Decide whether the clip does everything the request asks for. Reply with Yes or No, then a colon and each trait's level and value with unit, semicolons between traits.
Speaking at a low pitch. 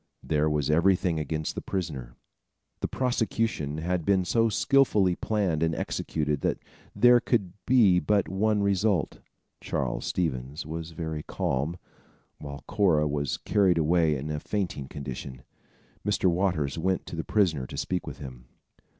Yes: very low, 85 Hz